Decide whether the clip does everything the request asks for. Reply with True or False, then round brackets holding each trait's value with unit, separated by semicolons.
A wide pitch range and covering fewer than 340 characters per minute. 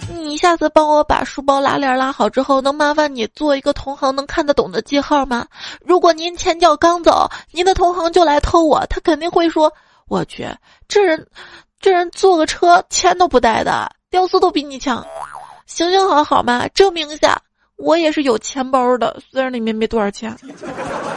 False (4.7 semitones; 270 characters per minute)